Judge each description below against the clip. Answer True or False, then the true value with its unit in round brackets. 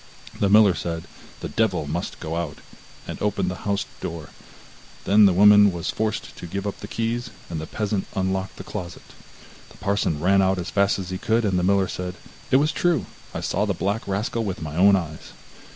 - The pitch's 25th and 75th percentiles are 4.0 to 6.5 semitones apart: False (2.8 semitones)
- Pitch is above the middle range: False (95 Hz)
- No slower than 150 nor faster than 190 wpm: False (205 wpm)